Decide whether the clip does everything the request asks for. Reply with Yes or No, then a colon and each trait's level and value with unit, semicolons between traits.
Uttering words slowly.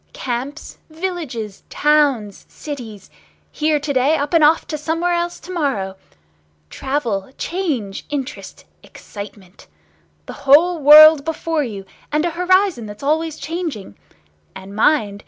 Yes: slow, 125 wpm